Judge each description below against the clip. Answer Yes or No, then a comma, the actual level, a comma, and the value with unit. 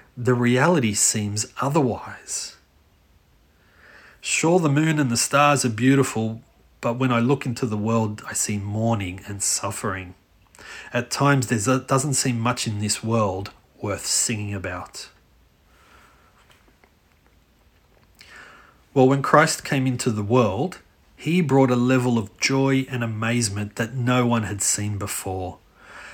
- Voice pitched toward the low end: Yes, low, 115 Hz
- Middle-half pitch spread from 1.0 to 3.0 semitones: No, average, 4.6 semitones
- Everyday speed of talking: No, slow, 130 wpm